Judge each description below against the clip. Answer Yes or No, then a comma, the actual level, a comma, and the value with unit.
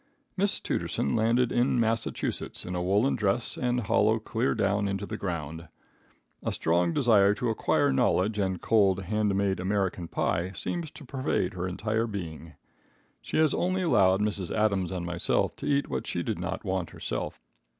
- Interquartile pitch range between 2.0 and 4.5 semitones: Yes, average, 3.9 semitones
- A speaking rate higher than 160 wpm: Yes, average, 170 wpm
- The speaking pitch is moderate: No, low, 100 Hz